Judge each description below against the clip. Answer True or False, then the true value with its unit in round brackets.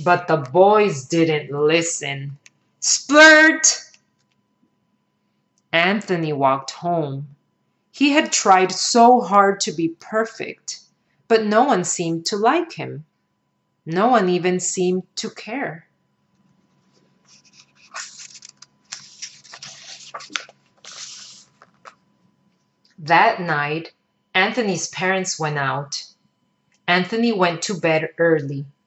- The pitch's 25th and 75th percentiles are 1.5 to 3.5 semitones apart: False (5.1 semitones)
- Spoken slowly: True (85 wpm)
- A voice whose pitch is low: False (180 Hz)